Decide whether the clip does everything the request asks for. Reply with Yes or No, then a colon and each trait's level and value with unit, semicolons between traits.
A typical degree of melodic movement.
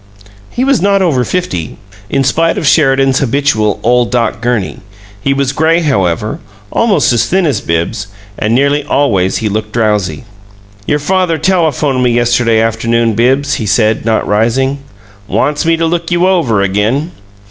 No: wide, 6.0 semitones